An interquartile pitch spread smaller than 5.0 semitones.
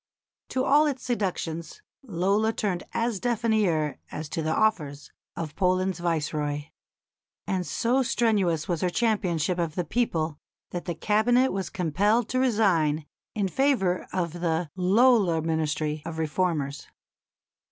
No: wide, 5.4 semitones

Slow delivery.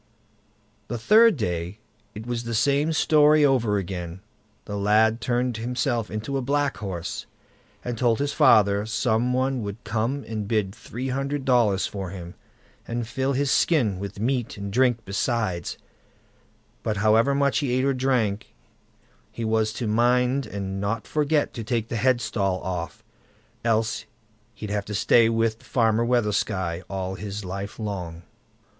No: average, 150 wpm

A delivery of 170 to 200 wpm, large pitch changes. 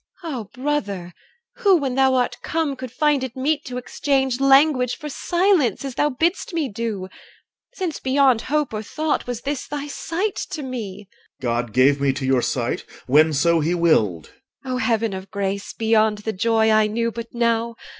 Yes: average, 185 wpm; wide, 6.0 semitones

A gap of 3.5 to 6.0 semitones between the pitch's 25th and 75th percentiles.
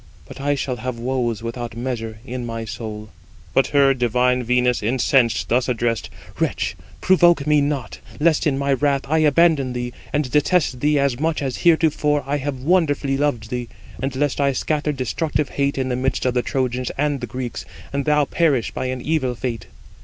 No: average, 3.0 semitones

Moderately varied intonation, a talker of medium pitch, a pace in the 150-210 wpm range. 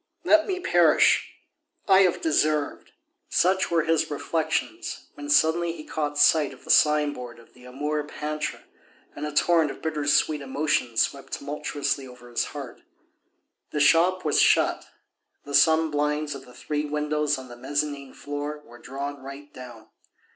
No: narrow, 1.9 semitones; medium, 150 Hz; average, 160 wpm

